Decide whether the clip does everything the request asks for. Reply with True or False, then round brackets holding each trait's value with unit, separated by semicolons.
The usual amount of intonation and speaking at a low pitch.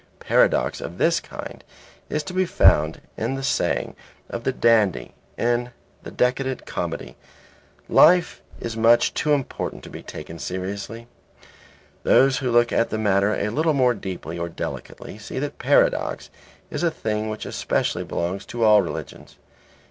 True (4.8 semitones; 115 Hz)